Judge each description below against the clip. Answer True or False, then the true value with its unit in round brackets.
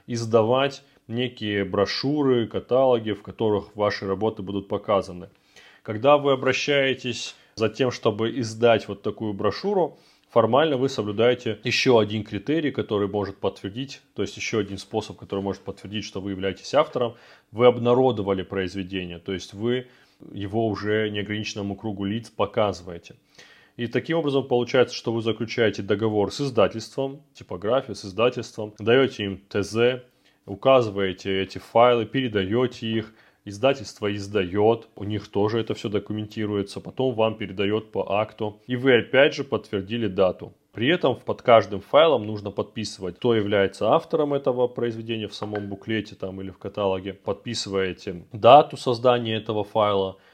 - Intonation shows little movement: False (3.3 semitones)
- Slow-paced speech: False (140 wpm)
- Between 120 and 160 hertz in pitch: False (110 Hz)